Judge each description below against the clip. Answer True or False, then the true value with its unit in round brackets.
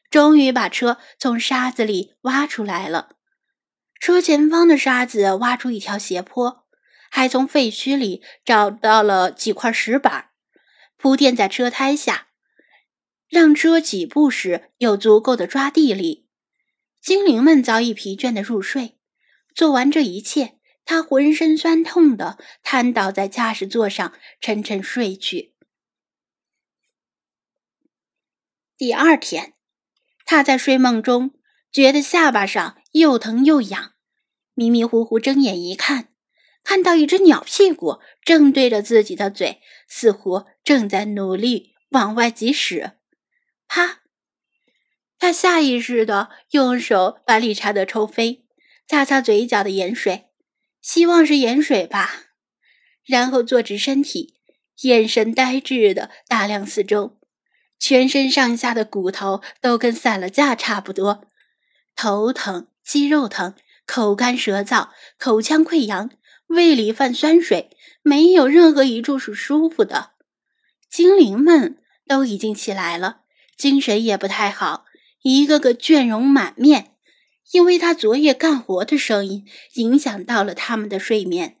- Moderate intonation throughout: False (5.7 semitones)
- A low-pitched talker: False (255 Hz)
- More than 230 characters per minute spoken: False (195 characters per minute)